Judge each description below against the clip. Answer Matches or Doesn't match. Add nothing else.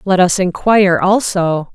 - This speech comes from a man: Doesn't match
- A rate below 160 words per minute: Matches